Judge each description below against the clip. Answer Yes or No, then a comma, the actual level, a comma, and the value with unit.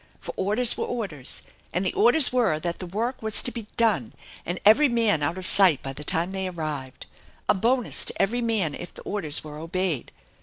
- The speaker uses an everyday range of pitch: No, wide, 6.1 semitones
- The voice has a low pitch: No, high, 190 Hz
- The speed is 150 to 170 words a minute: No, fast, 205 wpm